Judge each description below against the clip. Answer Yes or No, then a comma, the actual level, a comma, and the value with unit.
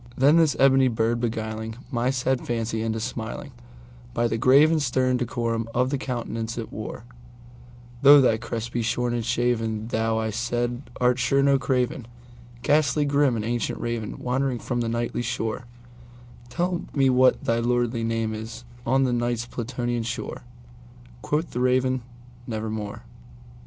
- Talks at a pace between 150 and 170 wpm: No, average, 140 wpm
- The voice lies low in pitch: Yes, low, 120 Hz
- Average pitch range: No, narrow, 1.9 semitones